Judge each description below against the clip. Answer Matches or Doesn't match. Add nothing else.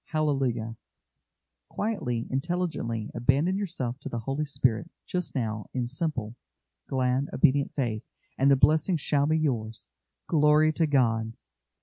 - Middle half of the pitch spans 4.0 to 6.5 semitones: Matches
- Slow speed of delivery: Matches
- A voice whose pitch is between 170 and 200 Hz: Doesn't match